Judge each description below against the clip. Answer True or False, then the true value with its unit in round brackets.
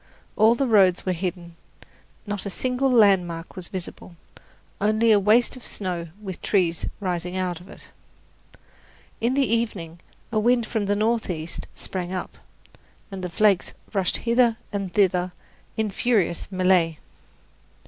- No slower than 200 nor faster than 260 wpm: False (140 wpm)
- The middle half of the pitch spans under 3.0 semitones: False (3.7 semitones)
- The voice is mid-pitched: False (195 Hz)